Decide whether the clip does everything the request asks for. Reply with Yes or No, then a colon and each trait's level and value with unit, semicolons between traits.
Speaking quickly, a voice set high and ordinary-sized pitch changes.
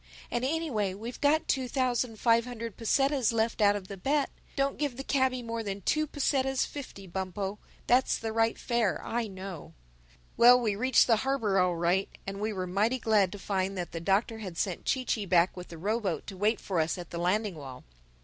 Yes: fast, 210 wpm; high, 220 Hz; average, 4.7 semitones